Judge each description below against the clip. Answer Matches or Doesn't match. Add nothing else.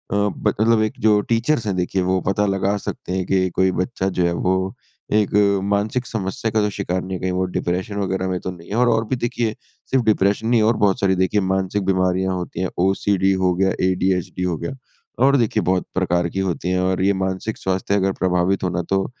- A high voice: Doesn't match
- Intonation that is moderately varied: Doesn't match